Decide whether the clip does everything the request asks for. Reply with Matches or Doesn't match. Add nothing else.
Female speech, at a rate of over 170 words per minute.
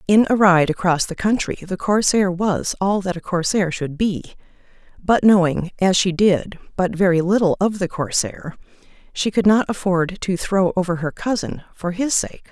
Matches